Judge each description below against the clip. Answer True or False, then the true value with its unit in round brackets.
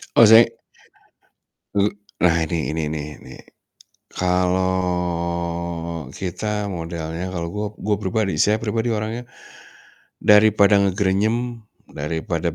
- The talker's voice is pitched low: True (95 Hz)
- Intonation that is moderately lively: True (3.9 semitones)